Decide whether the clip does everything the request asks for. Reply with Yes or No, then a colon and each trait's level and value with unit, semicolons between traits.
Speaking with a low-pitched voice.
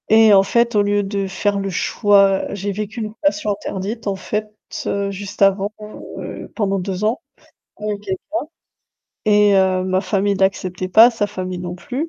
No: high, 200 Hz